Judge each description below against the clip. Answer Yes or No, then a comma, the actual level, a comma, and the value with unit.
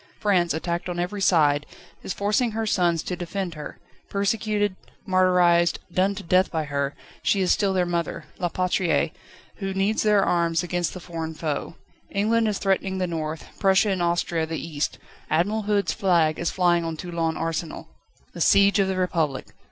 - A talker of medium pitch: Yes, medium, 180 Hz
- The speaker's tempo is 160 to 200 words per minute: Yes, average, 175 wpm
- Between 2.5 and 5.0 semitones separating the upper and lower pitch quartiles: Yes, average, 3.0 semitones